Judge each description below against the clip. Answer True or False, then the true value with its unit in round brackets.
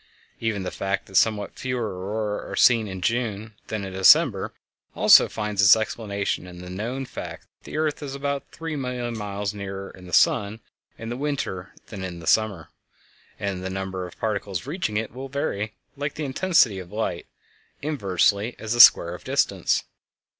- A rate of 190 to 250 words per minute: False (180 wpm)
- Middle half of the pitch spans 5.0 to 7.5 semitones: False (4.4 semitones)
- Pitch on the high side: False (105 Hz)